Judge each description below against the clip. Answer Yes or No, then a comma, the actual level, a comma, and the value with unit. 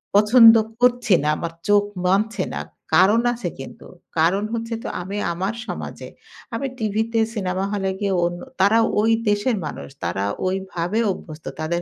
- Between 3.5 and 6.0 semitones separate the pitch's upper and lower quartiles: Yes, average, 3.9 semitones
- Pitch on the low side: No, high, 200 Hz